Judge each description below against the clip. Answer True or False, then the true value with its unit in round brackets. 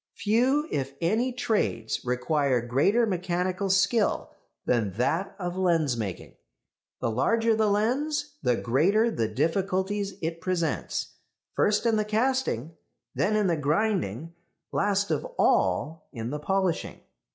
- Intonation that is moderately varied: False (6.6 semitones)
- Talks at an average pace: False (125 wpm)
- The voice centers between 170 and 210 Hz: True (185 Hz)